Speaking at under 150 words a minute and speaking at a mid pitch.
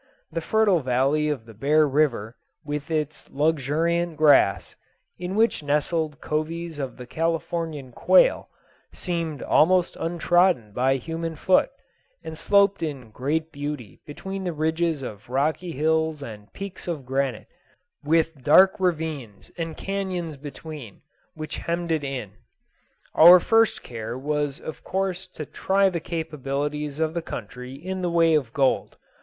Yes: average, 140 wpm; medium, 155 Hz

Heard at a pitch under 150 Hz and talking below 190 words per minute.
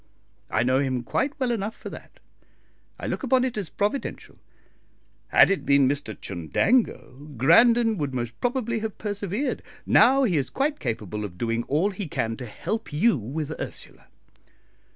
No: medium, 170 Hz; average, 160 wpm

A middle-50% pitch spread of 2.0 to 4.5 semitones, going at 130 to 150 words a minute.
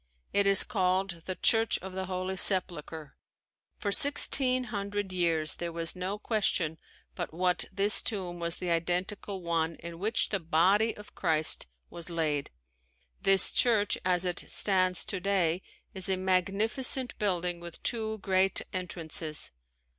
Yes: average, 2.8 semitones; average, 140 wpm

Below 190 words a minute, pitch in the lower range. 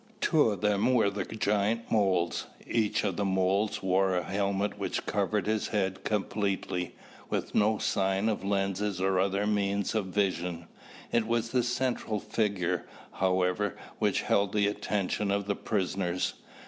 Yes: average, 150 wpm; low, 100 Hz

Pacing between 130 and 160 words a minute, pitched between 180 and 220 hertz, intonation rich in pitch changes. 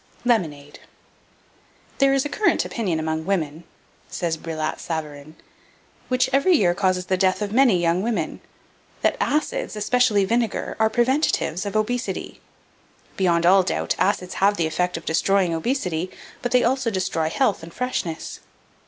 Yes: average, 145 wpm; high, 190 Hz; wide, 6.2 semitones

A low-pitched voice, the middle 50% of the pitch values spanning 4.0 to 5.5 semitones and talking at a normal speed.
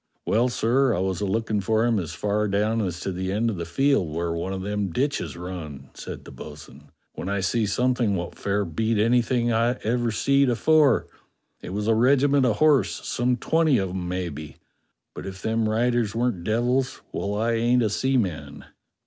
Yes: low, 110 Hz; average, 4.4 semitones; average, 190 wpm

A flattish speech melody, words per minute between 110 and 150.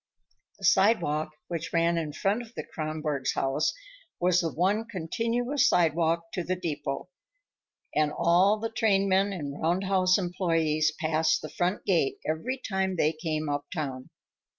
No: average, 3.8 semitones; average, 145 wpm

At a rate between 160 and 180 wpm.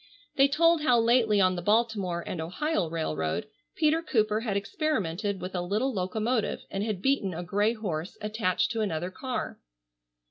Yes: average, 165 wpm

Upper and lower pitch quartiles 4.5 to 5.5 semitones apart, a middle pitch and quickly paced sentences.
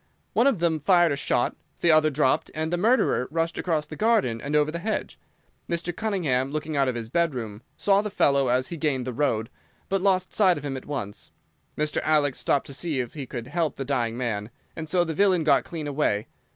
Yes: average, 4.8 semitones; medium, 150 Hz; fast, 220 wpm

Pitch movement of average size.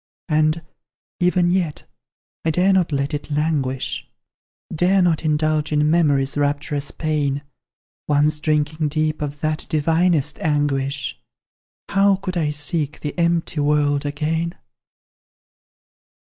No: narrow, 2.2 semitones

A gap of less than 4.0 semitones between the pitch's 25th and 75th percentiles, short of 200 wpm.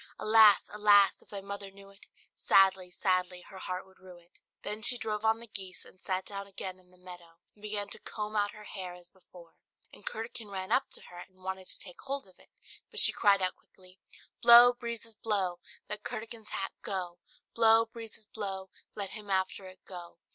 No: narrow, 2.6 semitones; fast, 205 wpm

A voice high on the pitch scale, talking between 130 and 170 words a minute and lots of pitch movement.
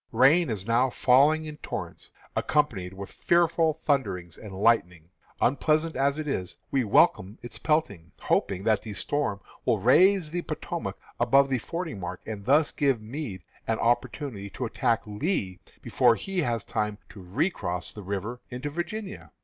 No: low, 120 Hz; average, 155 wpm; wide, 7.1 semitones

